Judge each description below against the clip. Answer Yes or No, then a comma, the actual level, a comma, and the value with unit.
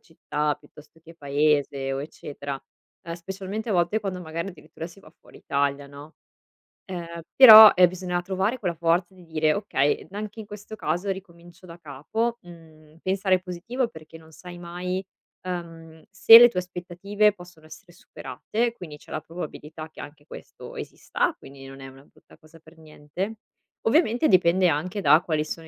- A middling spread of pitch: Yes, average, 3.6 semitones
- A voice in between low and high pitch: Yes, medium, 170 Hz